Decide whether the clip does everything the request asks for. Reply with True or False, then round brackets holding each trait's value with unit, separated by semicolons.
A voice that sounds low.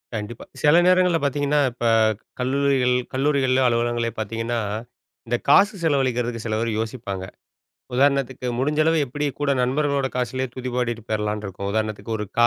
True (125 Hz)